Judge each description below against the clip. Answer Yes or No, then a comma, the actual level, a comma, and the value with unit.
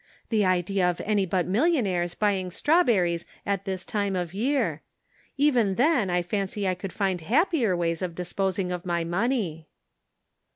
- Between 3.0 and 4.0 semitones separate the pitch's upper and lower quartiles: Yes, average, 3.4 semitones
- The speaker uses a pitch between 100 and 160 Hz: No, high, 190 Hz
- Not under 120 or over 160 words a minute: Yes, average, 155 wpm